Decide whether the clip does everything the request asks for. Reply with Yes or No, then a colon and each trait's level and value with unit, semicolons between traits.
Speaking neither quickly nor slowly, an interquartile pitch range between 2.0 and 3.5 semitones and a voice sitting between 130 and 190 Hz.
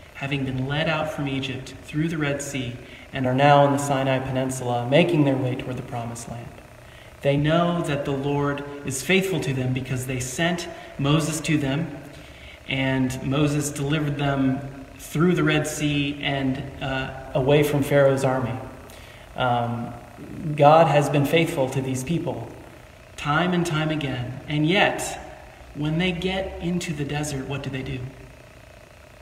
Yes: average, 160 wpm; narrow, 2.5 semitones; medium, 140 Hz